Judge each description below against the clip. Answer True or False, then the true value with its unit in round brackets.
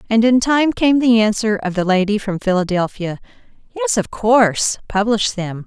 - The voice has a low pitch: False (215 Hz)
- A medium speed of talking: True (160 wpm)